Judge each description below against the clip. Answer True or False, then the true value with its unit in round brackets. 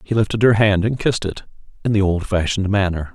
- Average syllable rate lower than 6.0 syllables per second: False (6.3 syllables/s)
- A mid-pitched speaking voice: False (100 Hz)